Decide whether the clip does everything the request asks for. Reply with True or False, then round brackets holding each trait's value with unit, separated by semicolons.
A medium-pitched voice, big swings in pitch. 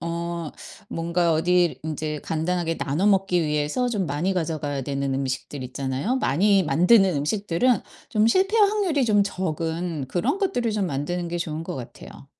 False (170 Hz; 4.8 semitones)